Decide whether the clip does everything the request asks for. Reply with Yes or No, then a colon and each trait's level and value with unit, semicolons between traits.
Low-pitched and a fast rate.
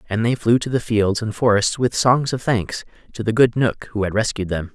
Yes: low, 110 Hz; fast, 255 wpm